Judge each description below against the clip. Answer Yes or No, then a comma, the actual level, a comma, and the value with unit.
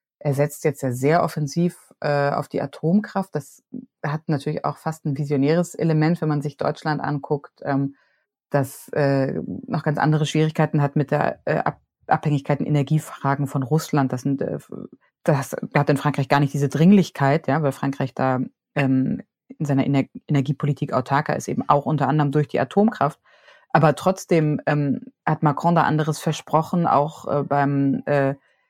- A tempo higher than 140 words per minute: Yes, average, 165 wpm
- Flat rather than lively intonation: Yes, narrow, 1.8 semitones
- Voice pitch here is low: No, medium, 150 Hz